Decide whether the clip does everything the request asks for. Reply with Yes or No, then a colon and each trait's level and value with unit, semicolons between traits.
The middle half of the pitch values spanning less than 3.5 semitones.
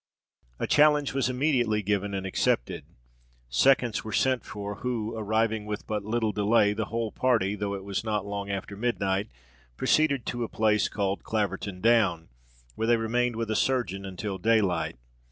Yes: average, 2.8 semitones